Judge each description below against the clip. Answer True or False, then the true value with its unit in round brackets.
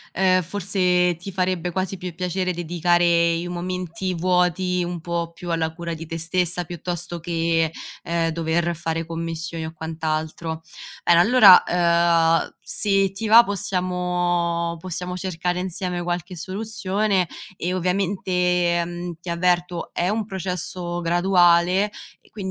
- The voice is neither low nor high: True (175 Hz)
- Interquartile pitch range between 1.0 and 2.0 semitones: True (1.5 semitones)